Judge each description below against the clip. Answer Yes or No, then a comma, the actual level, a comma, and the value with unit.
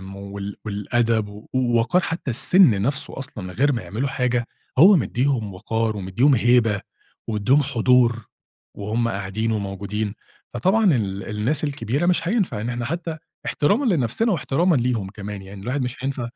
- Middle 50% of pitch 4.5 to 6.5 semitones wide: Yes, average, 5.0 semitones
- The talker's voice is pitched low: Yes, low, 120 Hz